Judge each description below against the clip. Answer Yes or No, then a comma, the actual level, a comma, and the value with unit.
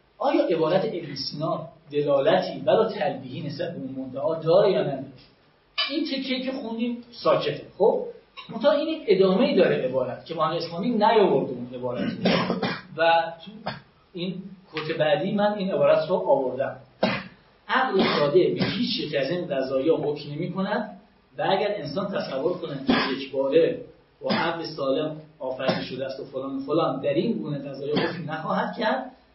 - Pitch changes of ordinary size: No, wide, 7.3 semitones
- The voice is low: No, medium, 170 Hz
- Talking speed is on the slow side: No, fast, 155 wpm